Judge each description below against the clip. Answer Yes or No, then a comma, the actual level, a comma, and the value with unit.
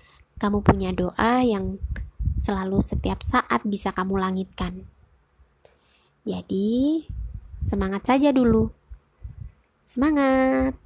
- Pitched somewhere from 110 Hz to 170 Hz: No, high, 190 Hz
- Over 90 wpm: No, slow, 85 wpm